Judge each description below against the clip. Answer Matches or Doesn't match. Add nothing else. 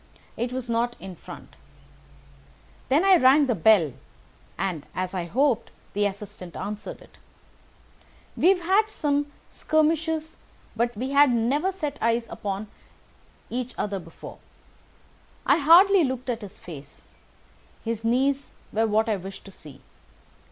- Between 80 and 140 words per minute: Matches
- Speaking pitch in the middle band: Doesn't match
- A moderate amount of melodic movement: Doesn't match